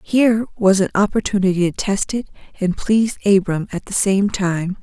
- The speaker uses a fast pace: No, average, 175 wpm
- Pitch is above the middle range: Yes, high, 200 Hz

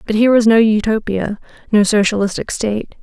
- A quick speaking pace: No, average, 160 wpm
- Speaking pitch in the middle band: No, high, 215 Hz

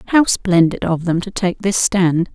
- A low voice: No, medium, 185 Hz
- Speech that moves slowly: No, fast, 205 wpm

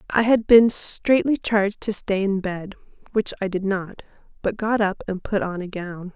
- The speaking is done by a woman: Yes, female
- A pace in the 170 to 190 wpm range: No, fast, 205 wpm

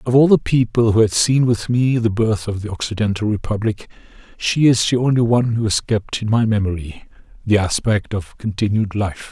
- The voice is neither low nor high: No, low, 110 Hz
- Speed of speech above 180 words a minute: Yes, average, 200 wpm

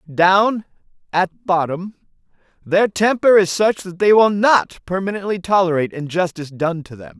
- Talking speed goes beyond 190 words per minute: No, average, 140 wpm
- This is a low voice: No, medium, 185 Hz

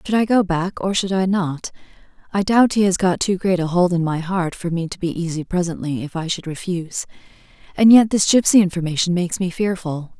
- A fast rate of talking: Yes, fast, 210 wpm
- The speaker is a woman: Yes, female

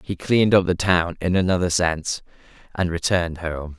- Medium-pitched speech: No, very low, 90 Hz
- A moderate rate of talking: Yes, average, 175 wpm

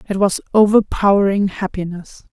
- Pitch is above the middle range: Yes, high, 195 Hz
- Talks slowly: Yes, slow, 100 wpm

